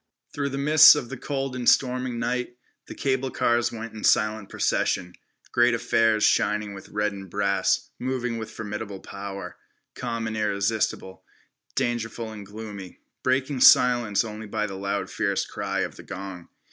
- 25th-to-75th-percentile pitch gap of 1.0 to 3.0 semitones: No, average, 3.4 semitones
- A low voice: Yes, low, 110 Hz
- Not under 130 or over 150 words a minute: No, average, 160 wpm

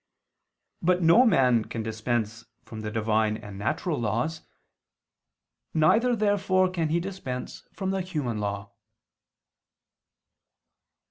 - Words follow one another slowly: Yes, slow, 110 wpm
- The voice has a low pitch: Yes, low, 130 Hz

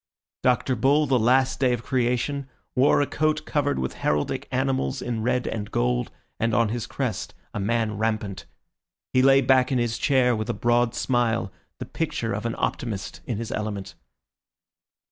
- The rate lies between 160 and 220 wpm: Yes, average, 170 wpm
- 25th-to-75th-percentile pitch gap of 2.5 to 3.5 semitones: Yes, average, 3.2 semitones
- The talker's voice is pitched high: No, low, 120 Hz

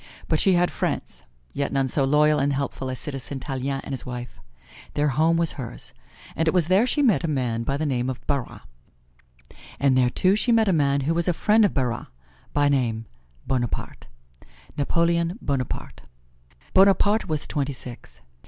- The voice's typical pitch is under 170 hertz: Yes, medium, 140 Hz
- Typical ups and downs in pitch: Yes, average, 4.4 semitones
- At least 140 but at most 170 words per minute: No, average, 180 wpm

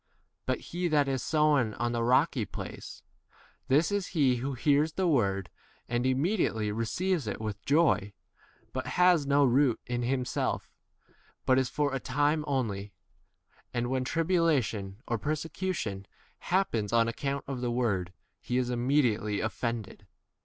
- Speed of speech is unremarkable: Yes, average, 155 wpm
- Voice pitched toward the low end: Yes, low, 130 Hz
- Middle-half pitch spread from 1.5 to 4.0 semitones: No, average, 4.5 semitones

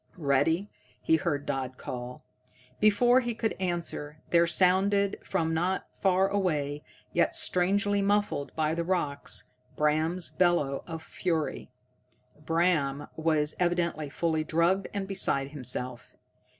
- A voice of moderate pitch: Yes, medium, 170 Hz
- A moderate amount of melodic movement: Yes, average, 4.3 semitones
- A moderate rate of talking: No, slow, 120 wpm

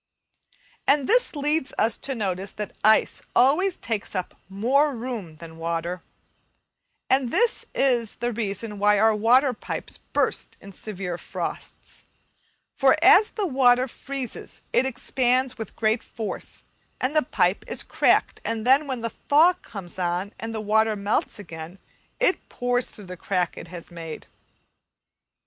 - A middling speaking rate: Yes, average, 150 wpm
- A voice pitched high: Yes, high, 225 Hz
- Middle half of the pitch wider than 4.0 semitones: Yes, average, 5.1 semitones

